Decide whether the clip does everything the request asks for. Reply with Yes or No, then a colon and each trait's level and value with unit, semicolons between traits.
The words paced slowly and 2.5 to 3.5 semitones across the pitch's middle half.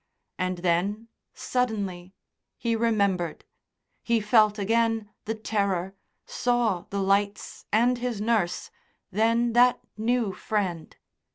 Yes: slow, 105 wpm; average, 3.1 semitones